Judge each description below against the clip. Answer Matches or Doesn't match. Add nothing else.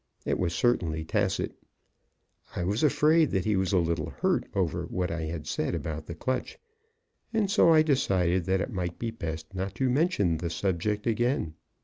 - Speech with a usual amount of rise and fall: Doesn't match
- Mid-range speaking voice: Doesn't match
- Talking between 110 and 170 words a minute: Doesn't match